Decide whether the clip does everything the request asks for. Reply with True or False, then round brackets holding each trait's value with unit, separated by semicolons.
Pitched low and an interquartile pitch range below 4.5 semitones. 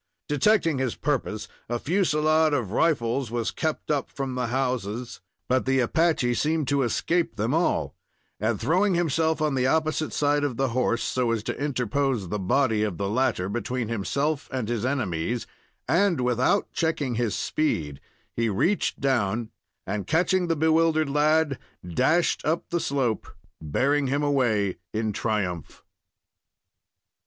False (130 Hz; 5.1 semitones)